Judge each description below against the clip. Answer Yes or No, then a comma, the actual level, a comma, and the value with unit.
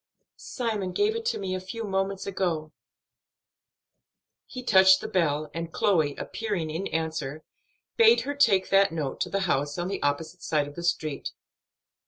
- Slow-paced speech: No, average, 165 wpm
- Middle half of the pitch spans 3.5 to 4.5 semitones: Yes, average, 4.1 semitones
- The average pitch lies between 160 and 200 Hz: Yes, medium, 185 Hz